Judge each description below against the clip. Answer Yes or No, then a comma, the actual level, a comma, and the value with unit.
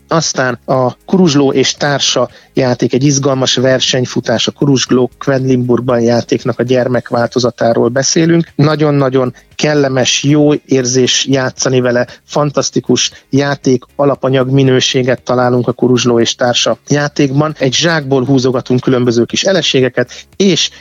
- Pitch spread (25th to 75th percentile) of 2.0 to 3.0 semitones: Yes, narrow, 2.4 semitones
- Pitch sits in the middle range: No, low, 130 Hz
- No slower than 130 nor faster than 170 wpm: No, average, 110 wpm